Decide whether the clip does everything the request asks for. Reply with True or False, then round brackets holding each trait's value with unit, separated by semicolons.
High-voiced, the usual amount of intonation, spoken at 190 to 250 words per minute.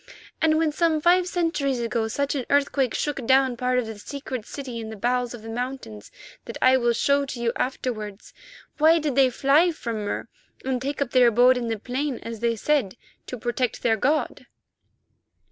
True (255 Hz; 3.3 semitones; 195 wpm)